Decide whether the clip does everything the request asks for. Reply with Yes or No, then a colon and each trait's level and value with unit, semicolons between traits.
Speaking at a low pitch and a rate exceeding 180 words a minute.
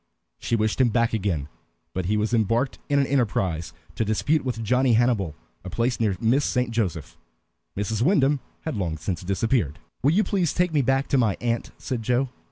Yes: low, 115 Hz; average, 190 wpm